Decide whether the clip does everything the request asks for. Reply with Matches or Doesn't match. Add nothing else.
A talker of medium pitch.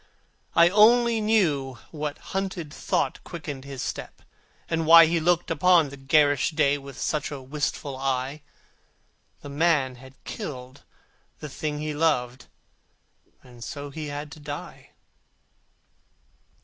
Matches